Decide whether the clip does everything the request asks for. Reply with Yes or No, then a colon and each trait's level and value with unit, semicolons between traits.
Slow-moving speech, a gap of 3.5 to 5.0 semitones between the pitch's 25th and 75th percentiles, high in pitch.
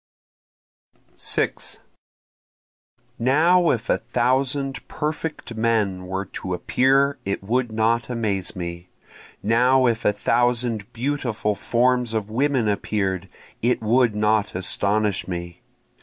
No: slow, 110 wpm; average, 3.8 semitones; low, 115 Hz